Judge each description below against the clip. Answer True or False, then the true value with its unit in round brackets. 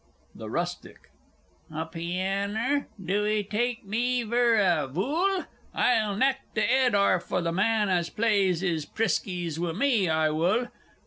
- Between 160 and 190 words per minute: False (145 wpm)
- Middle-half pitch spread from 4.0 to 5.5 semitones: True (5.2 semitones)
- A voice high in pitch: True (200 Hz)